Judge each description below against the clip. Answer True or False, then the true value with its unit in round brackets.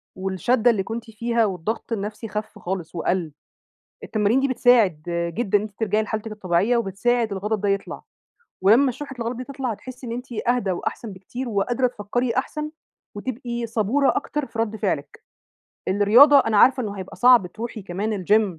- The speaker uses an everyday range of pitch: True (3.5 semitones)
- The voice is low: False (220 Hz)